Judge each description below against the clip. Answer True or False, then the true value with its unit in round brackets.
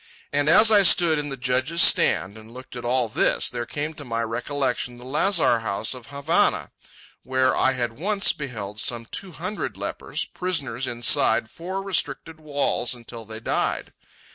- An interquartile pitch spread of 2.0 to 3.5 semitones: False (5.1 semitones)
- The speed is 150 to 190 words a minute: True (165 wpm)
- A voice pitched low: True (130 Hz)